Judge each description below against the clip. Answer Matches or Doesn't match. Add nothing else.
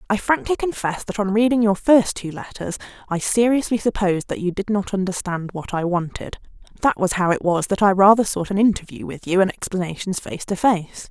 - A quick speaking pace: Matches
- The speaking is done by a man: Doesn't match